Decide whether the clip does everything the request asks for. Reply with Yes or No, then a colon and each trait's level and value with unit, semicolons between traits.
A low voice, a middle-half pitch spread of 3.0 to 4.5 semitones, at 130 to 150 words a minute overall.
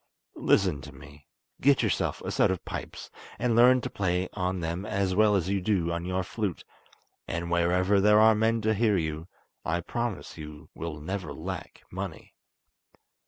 No: very low, 95 Hz; average, 3.9 semitones; average, 170 wpm